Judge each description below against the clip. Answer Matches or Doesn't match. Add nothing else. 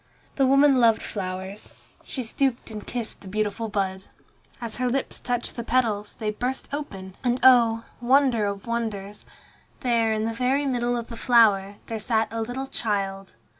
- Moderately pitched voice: Doesn't match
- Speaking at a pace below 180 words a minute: Matches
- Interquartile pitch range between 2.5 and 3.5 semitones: Matches